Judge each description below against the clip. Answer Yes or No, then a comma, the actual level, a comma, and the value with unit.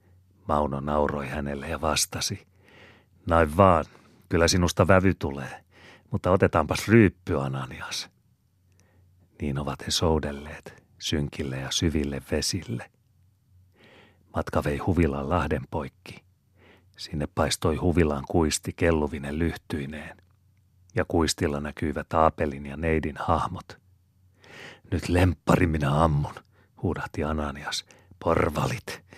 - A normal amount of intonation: Yes, average, 4.1 semitones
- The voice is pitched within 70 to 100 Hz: Yes, very low, 85 Hz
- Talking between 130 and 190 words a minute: No, average, 100 wpm